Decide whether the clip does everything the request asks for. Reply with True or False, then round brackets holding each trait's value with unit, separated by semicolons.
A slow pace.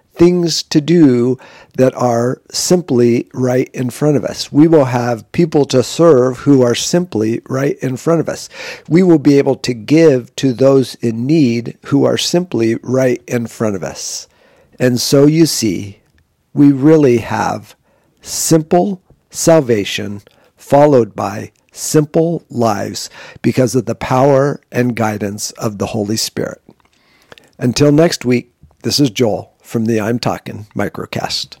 False (145 wpm)